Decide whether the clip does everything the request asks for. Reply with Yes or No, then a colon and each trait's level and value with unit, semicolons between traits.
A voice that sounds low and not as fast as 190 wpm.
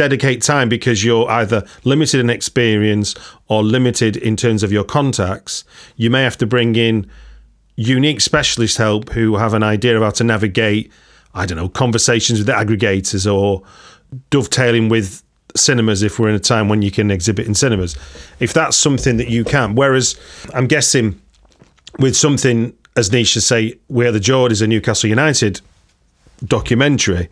Yes: low, 115 Hz; average, 165 wpm